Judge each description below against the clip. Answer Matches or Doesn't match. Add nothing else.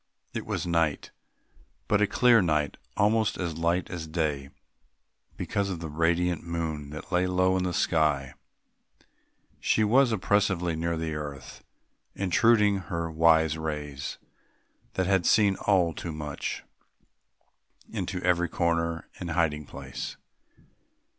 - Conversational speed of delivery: Doesn't match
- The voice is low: Matches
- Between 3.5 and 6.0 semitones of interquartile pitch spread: Doesn't match